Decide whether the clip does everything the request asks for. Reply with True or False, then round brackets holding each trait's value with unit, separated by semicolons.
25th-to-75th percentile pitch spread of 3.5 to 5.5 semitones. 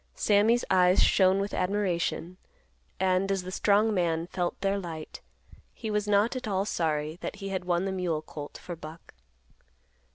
False (2.8 semitones)